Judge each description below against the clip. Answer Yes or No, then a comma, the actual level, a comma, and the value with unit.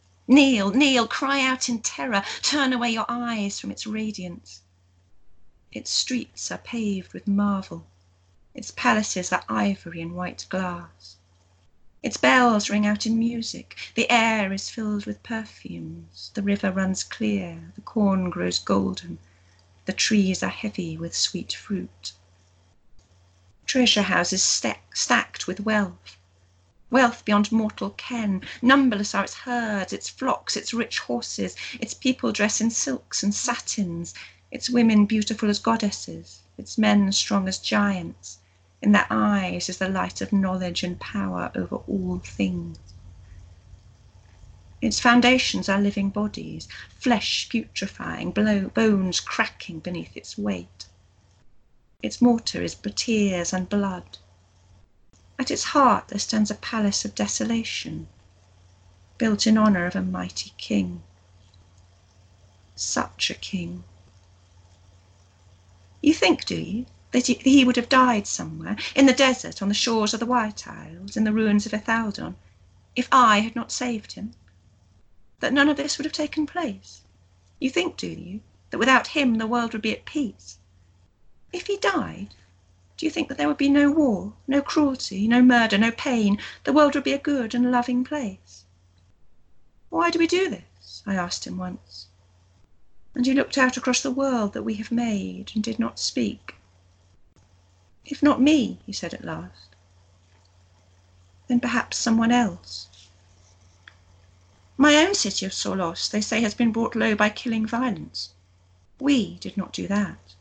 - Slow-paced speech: No, average, 150 wpm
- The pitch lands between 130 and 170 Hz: No, high, 190 Hz